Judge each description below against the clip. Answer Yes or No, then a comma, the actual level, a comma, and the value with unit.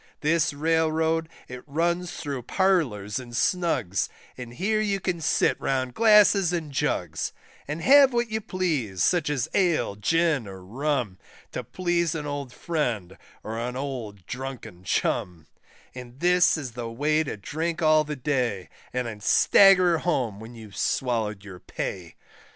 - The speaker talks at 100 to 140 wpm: No, average, 150 wpm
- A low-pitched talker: No, medium, 145 Hz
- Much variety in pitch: Yes, wide, 6.6 semitones